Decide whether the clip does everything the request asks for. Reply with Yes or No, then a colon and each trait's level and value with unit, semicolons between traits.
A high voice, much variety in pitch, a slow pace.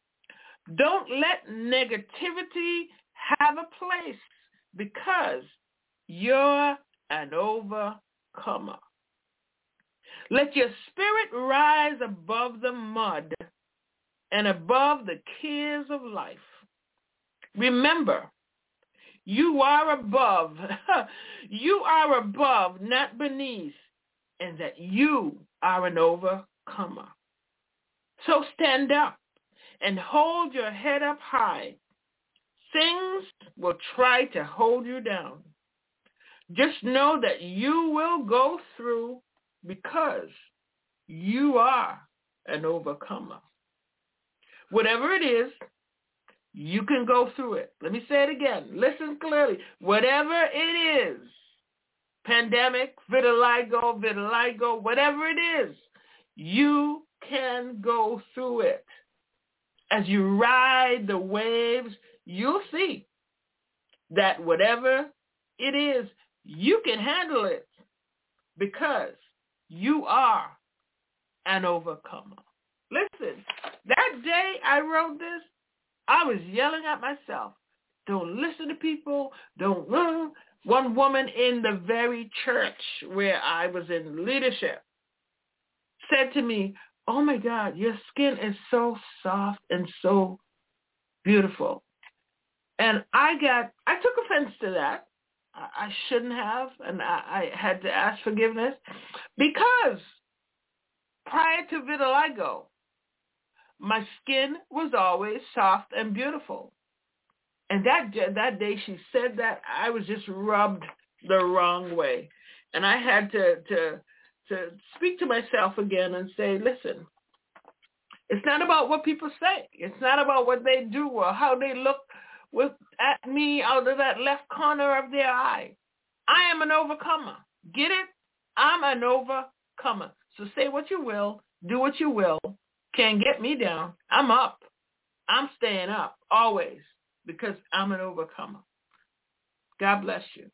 Yes: very high, 260 Hz; wide, 5.8 semitones; slow, 115 wpm